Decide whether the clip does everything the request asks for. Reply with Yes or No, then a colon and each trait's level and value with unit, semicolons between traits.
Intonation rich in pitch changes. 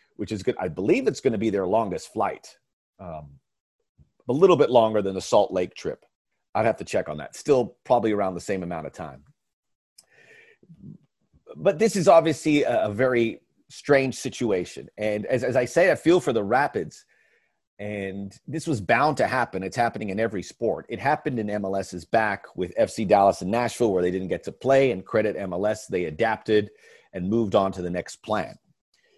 Yes: wide, 7.7 semitones